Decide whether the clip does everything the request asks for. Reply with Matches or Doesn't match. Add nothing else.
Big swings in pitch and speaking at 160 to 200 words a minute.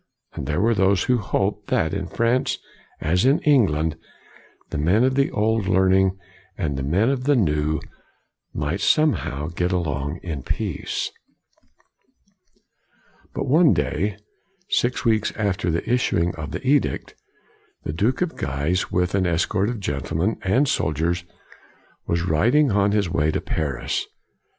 Doesn't match